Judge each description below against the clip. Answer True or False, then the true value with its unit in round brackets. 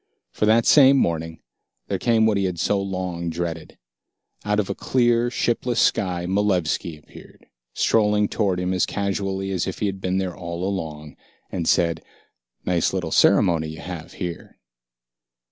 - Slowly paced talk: False (160 wpm)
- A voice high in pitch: False (95 Hz)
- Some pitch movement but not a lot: True (3.4 semitones)